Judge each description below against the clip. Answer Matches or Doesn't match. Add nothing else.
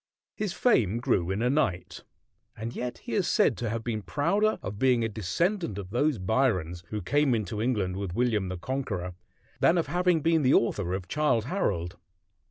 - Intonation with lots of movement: Matches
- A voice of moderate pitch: Doesn't match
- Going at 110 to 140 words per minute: Doesn't match